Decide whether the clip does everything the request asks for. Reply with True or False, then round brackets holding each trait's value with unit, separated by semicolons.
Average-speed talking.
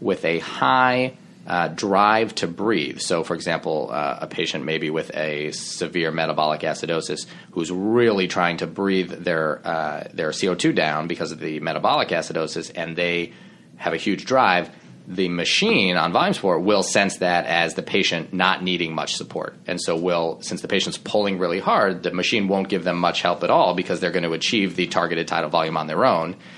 True (190 wpm)